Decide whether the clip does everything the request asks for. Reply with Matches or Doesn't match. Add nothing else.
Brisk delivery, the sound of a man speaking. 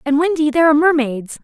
Doesn't match